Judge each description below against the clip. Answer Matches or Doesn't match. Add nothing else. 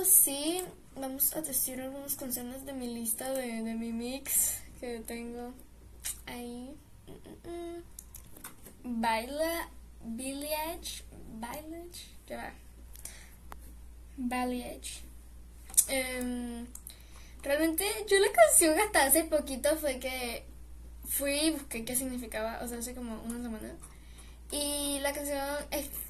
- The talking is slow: Matches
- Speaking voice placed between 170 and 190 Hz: Doesn't match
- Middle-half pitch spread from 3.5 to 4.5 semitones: Matches